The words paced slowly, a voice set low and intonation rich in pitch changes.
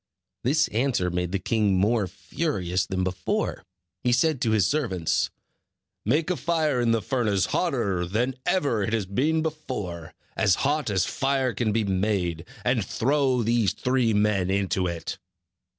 No: average, 155 wpm; low, 110 Hz; wide, 5.9 semitones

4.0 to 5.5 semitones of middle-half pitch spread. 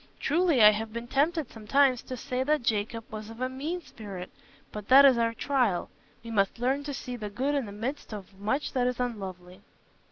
Yes: average, 4.3 semitones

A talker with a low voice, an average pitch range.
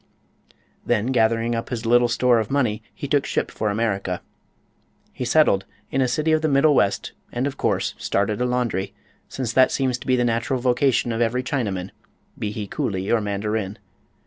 Yes: low, 120 Hz; average, 3.4 semitones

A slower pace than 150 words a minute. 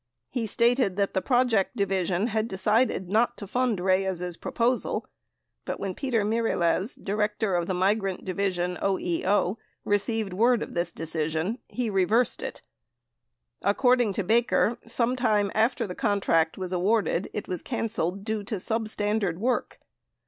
Yes: average, 140 wpm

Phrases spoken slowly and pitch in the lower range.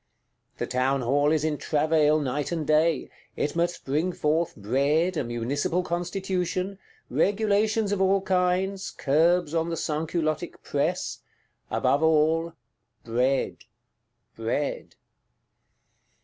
No: slow, 105 wpm; medium, 160 Hz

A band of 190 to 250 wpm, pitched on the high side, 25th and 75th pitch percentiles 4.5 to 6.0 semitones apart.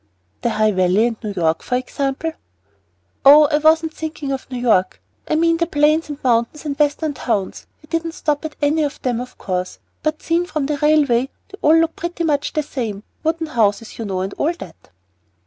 Yes: fast, 205 wpm; very high, 290 Hz; average, 5.3 semitones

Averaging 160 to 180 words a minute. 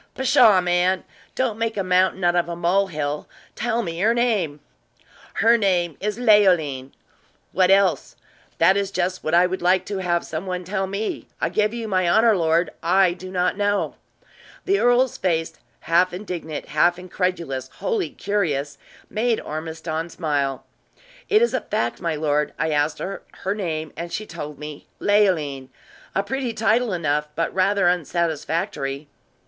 Yes: average, 165 wpm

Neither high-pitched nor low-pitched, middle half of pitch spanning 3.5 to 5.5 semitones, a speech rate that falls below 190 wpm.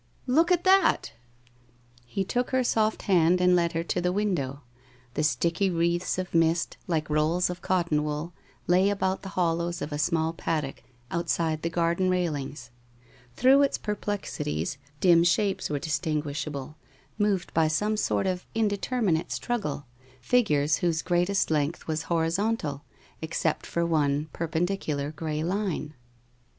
Yes: medium, 170 Hz; average, 3.8 semitones; average, 150 wpm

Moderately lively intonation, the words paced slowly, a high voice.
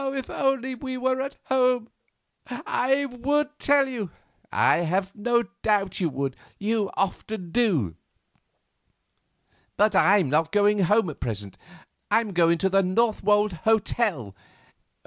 No: wide, 5.7 semitones; slow, 125 wpm; high, 210 Hz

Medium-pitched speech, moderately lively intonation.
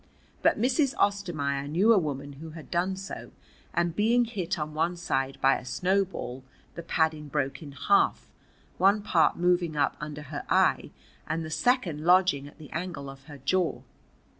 Yes: medium, 165 Hz; average, 4.7 semitones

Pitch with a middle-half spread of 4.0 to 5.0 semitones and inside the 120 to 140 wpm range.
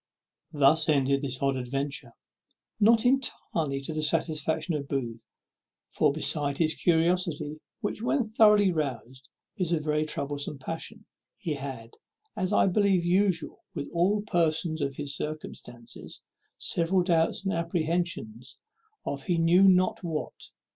Yes: average, 4.3 semitones; slow, 135 wpm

